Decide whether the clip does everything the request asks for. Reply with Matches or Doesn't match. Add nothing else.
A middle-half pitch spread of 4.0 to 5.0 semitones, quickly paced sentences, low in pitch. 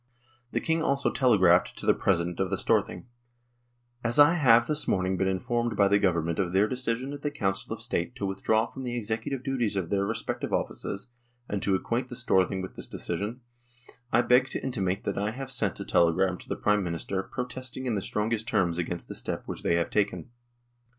Matches